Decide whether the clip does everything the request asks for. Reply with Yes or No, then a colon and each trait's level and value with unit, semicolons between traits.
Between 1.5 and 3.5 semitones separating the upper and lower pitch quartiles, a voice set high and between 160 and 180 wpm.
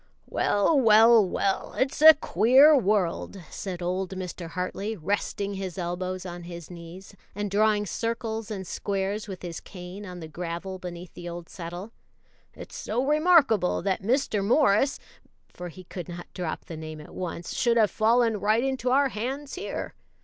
No: average, 4.3 semitones; high, 195 Hz; average, 165 wpm